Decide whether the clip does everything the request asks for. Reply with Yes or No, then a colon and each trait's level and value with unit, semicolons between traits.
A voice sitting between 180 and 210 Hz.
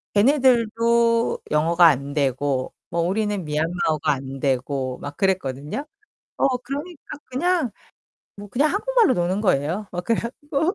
Yes: high, 190 Hz